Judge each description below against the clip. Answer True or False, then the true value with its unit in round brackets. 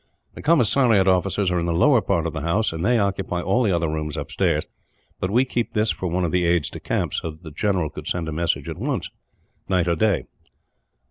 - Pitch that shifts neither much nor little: True (3.9 semitones)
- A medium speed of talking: False (230 wpm)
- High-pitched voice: False (90 Hz)